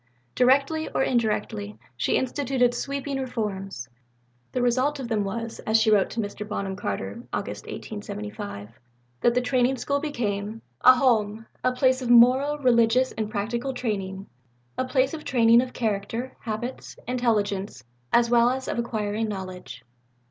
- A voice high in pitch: Yes, high, 235 Hz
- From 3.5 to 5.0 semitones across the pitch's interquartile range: Yes, average, 3.8 semitones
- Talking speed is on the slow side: No, average, 150 wpm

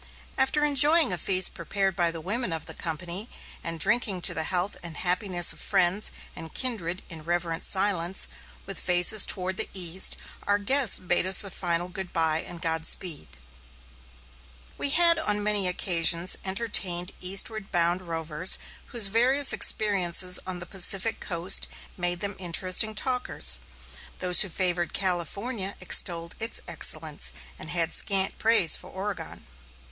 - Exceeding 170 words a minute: No, average, 145 wpm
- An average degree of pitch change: Yes, average, 3.0 semitones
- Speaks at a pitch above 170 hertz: Yes, medium, 185 Hz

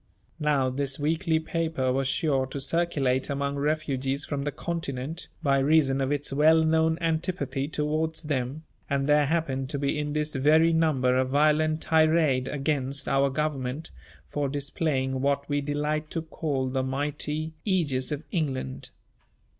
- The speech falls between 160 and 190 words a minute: No, average, 150 wpm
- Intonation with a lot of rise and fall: No, narrow, 2.6 semitones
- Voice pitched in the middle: Yes, medium, 145 Hz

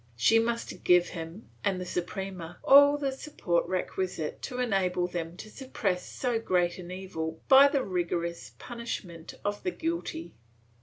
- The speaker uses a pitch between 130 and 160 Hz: No, high, 190 Hz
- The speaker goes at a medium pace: Yes, average, 150 wpm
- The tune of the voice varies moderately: No, wide, 5.9 semitones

